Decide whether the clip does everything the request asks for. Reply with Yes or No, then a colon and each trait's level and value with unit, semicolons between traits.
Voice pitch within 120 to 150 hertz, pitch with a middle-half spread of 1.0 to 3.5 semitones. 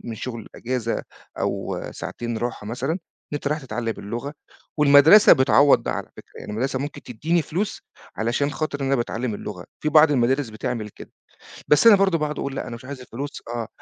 No: low, 135 Hz; average, 4.0 semitones